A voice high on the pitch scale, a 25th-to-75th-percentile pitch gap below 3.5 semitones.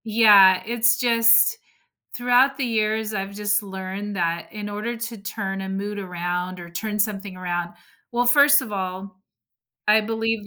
Yes: high, 210 Hz; average, 3.1 semitones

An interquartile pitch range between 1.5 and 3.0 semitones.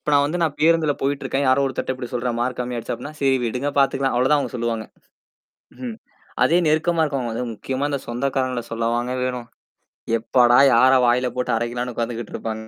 Yes: narrow, 2.6 semitones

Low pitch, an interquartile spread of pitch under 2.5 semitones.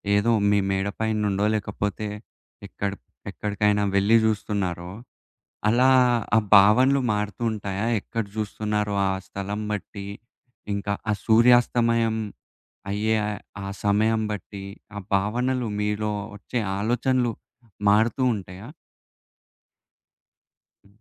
Yes: low, 105 Hz; narrow, 2.0 semitones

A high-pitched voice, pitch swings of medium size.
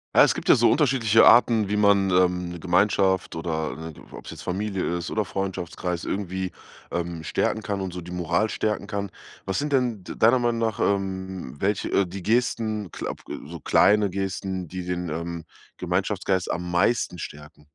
No: very low, 95 Hz; average, 3.1 semitones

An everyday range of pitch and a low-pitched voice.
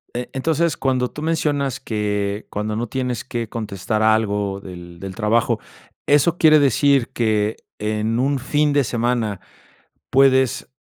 Yes: average, 4.4 semitones; low, 120 Hz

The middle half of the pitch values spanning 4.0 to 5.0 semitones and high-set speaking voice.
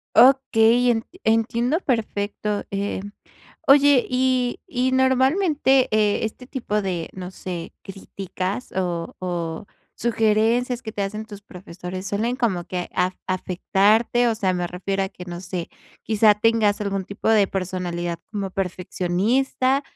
Yes: average, 4.7 semitones; high, 210 Hz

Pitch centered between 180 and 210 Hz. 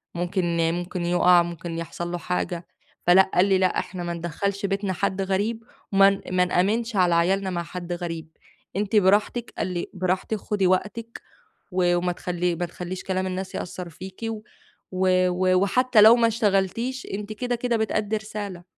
Yes: medium, 185 Hz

